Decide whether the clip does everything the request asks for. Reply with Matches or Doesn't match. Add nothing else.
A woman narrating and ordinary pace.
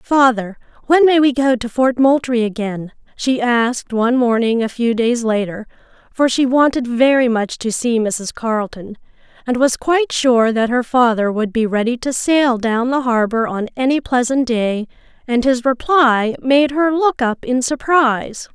Matches